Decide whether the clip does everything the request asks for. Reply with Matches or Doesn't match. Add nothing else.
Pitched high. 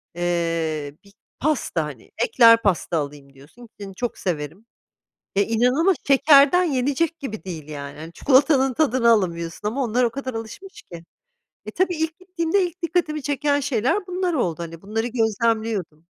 Matches